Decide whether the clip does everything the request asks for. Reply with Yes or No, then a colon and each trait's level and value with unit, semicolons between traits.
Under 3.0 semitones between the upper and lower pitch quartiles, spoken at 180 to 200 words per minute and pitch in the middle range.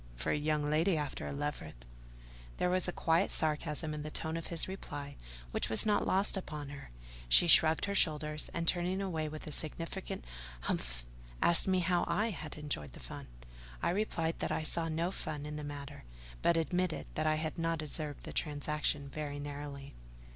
Yes: narrow, 2.6 semitones; average, 190 wpm; medium, 155 Hz